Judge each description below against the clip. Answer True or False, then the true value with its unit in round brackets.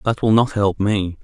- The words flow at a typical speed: False (245 wpm)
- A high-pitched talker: False (105 Hz)